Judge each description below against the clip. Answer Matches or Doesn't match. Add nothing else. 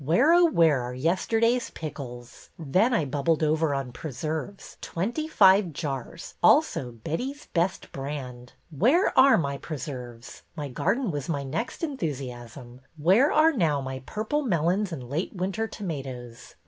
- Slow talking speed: Doesn't match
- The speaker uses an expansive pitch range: Matches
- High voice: Doesn't match